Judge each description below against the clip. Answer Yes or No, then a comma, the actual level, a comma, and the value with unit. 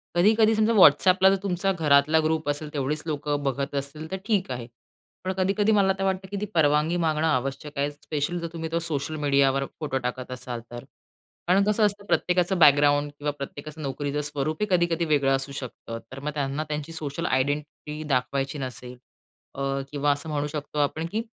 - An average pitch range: Yes, average, 3.6 semitones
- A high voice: No, medium, 150 Hz